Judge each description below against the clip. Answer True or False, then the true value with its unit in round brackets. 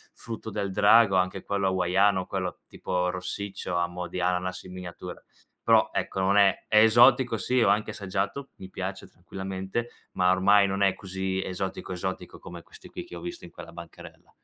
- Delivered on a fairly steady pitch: True (1.8 semitones)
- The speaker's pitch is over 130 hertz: False (95 Hz)